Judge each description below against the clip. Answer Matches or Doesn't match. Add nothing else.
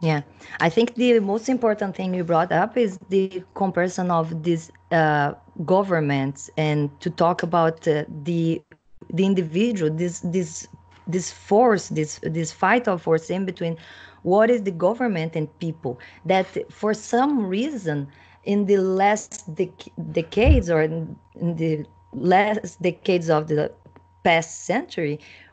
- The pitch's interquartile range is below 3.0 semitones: Doesn't match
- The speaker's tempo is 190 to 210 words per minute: Doesn't match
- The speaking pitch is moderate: Matches